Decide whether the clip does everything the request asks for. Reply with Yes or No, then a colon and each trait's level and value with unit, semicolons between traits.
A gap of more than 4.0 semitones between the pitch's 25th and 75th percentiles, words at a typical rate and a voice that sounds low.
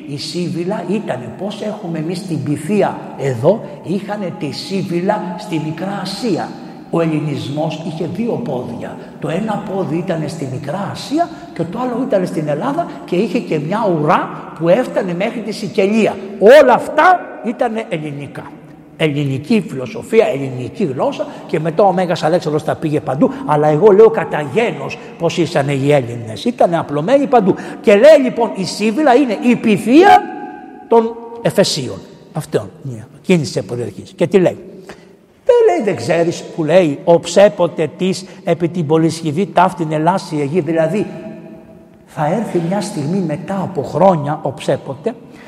No: average, 5.3 semitones; average, 150 wpm; medium, 180 Hz